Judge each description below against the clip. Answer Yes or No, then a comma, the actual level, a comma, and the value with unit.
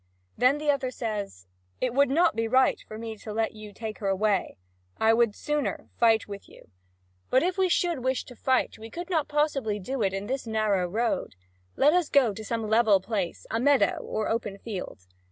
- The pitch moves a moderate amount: Yes, average, 4.2 semitones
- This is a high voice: Yes, high, 225 Hz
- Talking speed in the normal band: No, fast, 210 wpm